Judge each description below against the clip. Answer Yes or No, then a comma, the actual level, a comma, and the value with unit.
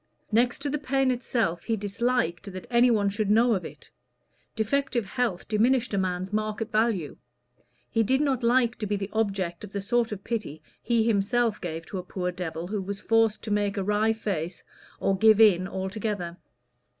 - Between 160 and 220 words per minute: Yes, average, 185 wpm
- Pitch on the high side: Yes, high, 210 Hz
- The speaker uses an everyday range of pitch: Yes, average, 3.5 semitones